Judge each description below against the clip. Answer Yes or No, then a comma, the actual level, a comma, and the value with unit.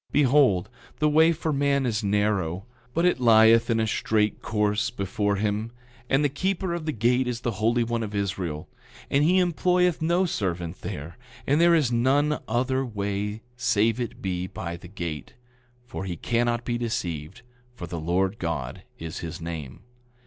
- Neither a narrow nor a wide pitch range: No, wide, 6.1 semitones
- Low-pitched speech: Yes, low, 110 Hz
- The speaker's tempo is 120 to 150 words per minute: No, average, 170 wpm